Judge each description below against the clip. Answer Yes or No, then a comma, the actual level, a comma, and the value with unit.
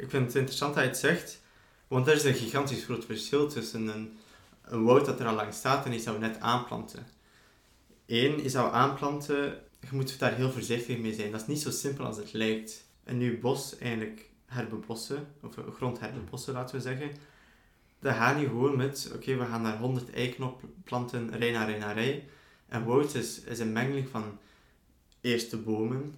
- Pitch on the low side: Yes, low, 125 Hz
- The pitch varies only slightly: No, average, 3.2 semitones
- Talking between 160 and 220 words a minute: Yes, fast, 200 wpm